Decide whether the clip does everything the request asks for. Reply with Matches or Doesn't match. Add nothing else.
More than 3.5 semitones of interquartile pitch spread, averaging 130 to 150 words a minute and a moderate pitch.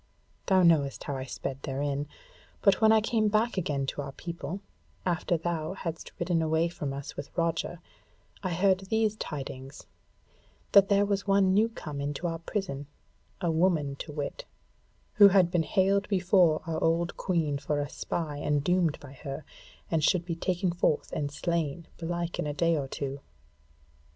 Doesn't match